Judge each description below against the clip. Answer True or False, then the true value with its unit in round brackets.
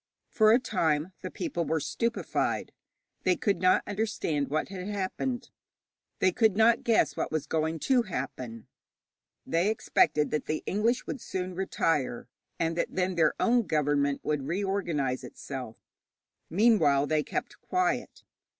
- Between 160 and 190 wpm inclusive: False (140 wpm)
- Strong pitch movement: True (6.2 semitones)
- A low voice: False (180 Hz)